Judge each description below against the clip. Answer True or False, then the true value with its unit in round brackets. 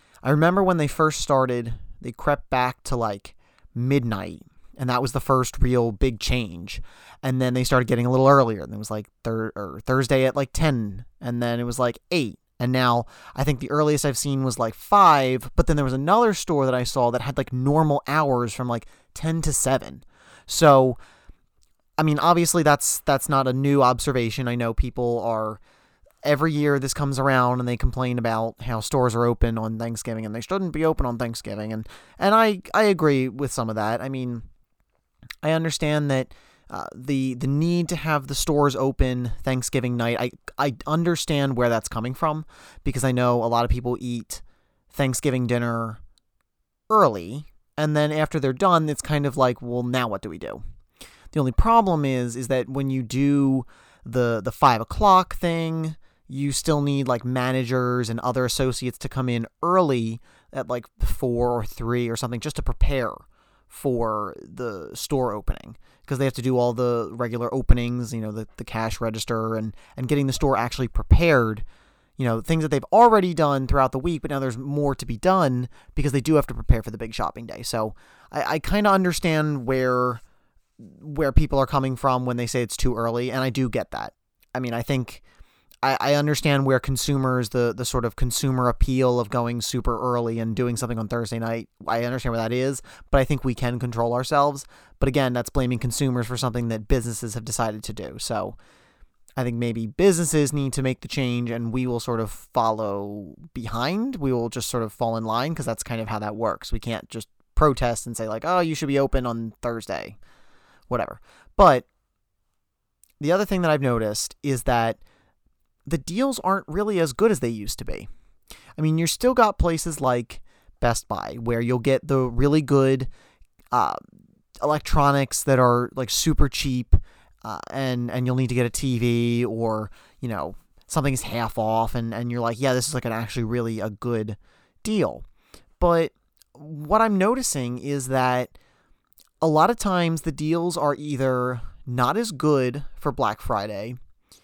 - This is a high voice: False (125 Hz)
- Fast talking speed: False (195 wpm)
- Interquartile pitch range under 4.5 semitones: True (3.3 semitones)